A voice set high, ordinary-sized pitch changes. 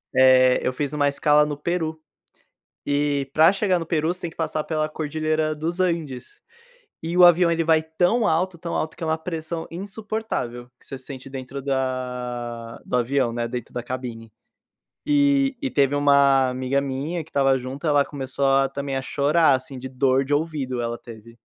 No: medium, 145 Hz; average, 3.8 semitones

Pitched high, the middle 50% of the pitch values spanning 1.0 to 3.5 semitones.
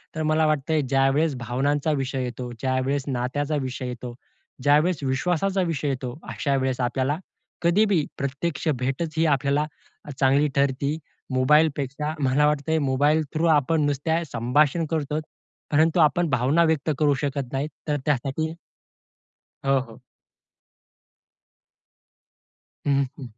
No: medium, 145 Hz; average, 2.8 semitones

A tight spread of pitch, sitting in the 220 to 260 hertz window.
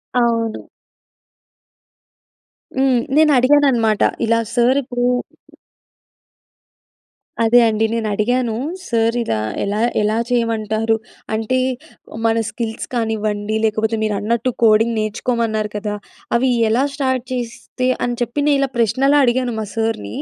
Yes: narrow, 2.3 semitones; high, 230 Hz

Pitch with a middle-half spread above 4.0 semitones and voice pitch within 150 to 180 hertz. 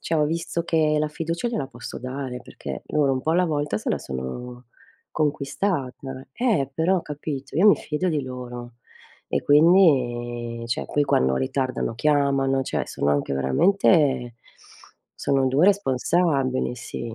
No: average, 4.4 semitones; medium, 140 Hz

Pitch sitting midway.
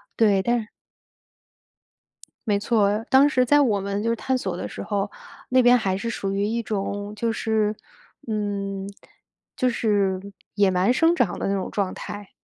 No: high, 210 Hz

